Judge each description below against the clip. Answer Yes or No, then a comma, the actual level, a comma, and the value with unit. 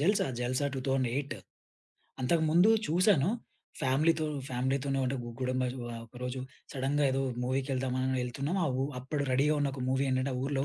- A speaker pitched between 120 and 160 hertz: Yes, low, 135 Hz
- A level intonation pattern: Yes, narrow, 2.0 semitones